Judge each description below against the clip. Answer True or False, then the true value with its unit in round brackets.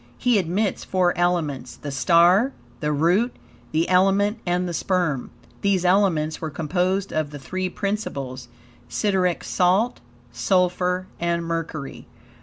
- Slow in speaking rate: True (125 wpm)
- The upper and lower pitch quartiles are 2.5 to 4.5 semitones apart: True (3.4 semitones)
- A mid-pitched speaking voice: True (180 Hz)